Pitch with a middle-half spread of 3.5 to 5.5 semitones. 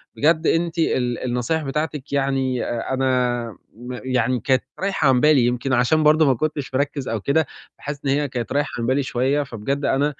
No: average, 3.0 semitones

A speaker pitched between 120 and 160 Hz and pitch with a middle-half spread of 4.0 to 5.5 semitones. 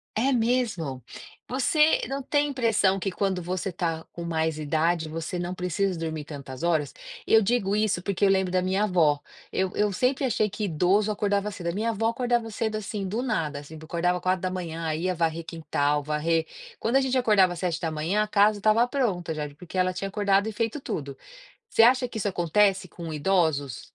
No: medium, 185 Hz; average, 4.6 semitones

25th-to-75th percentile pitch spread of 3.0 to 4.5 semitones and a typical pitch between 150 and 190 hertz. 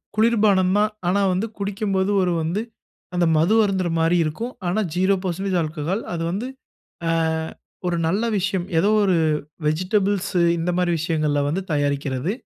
Yes: average, 3.4 semitones; medium, 185 Hz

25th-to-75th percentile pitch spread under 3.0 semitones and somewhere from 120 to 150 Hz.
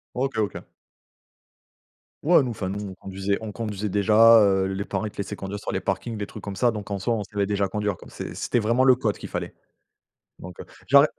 No: narrow, 2.6 semitones; low, 105 Hz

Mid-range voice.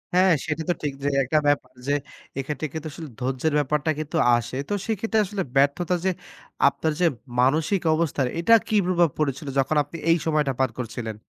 Yes: medium, 155 Hz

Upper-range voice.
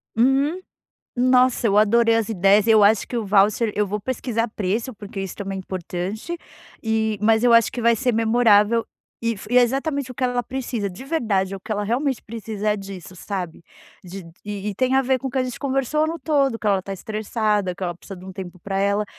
Yes: high, 220 Hz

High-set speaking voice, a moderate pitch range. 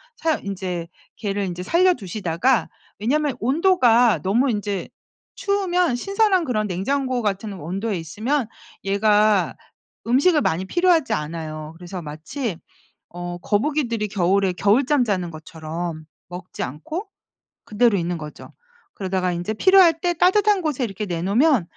No: high, 210 Hz; wide, 8.0 semitones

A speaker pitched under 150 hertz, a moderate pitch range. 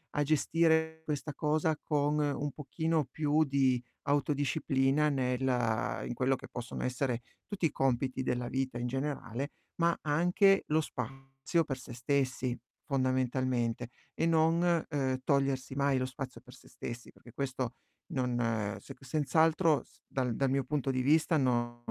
Yes: low, 135 Hz; average, 3.0 semitones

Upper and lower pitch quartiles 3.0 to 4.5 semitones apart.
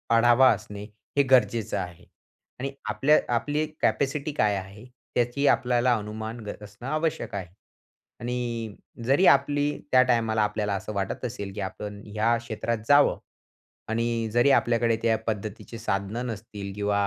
Yes: average, 3.3 semitones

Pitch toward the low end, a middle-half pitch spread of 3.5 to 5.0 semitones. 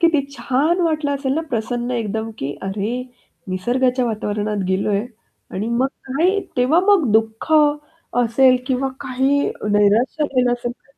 No: high, 245 Hz; average, 4.1 semitones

